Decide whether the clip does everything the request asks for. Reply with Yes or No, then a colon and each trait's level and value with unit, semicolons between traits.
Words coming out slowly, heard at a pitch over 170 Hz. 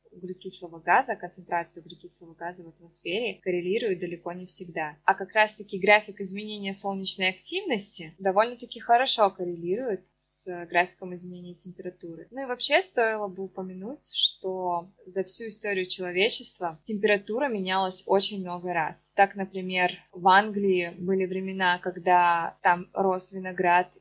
No: average, 130 wpm; medium, 185 Hz